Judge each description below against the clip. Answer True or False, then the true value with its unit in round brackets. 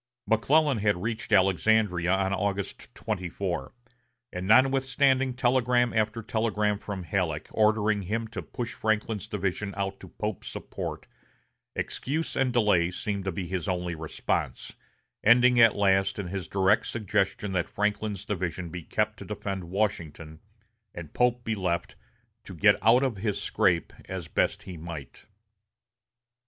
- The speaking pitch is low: True (100 Hz)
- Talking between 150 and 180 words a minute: False (140 wpm)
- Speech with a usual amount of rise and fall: True (3.6 semitones)